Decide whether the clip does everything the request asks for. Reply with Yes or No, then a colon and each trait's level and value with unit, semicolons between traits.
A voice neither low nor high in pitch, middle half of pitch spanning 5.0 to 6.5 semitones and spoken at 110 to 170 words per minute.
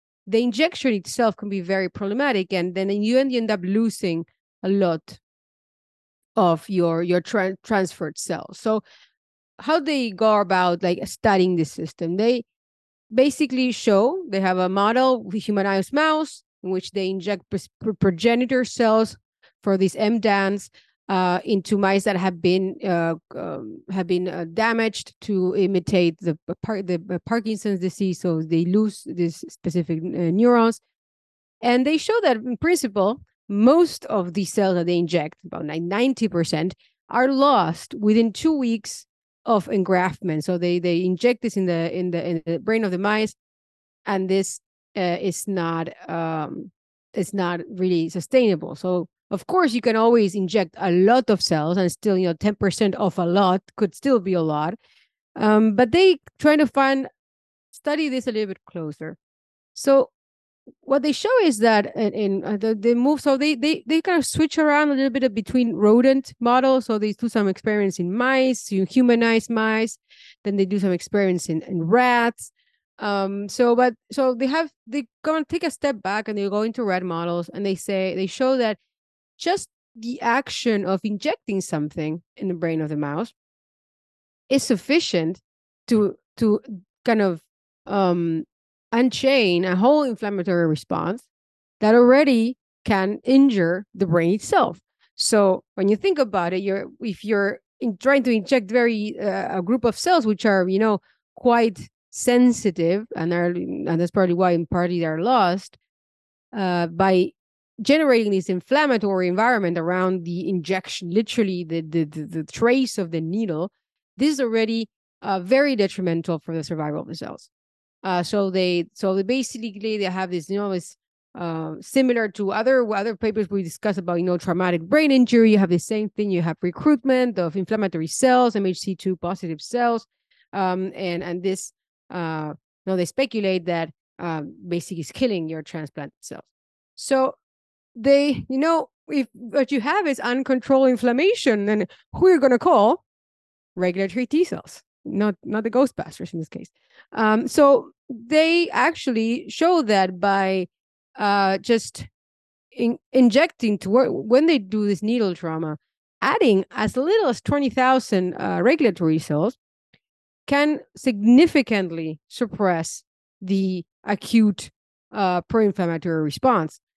No: high, 205 Hz; wide, 5.4 semitones; average, 160 wpm